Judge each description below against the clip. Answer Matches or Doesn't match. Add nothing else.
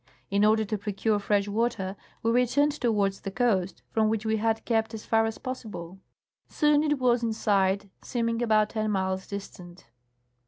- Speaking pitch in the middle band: Doesn't match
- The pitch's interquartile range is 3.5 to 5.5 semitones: Doesn't match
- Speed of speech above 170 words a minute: Matches